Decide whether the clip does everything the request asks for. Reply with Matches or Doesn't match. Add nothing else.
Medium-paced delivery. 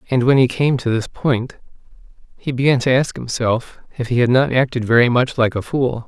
Doesn't match